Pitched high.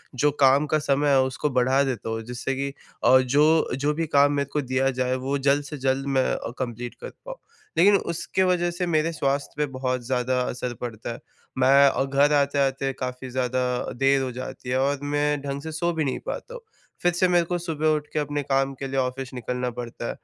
No: low, 135 Hz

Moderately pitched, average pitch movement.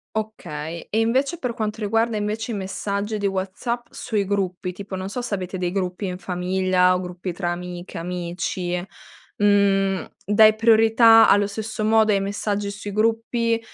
No: high, 200 Hz; average, 3.2 semitones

